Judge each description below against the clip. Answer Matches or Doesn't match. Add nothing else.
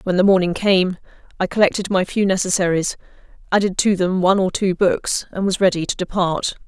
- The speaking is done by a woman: Matches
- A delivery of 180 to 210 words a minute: Matches